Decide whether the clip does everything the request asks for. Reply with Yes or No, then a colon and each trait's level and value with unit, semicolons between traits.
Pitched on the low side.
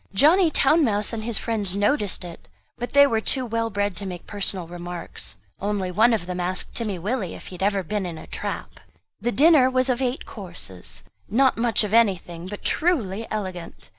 No: high, 210 Hz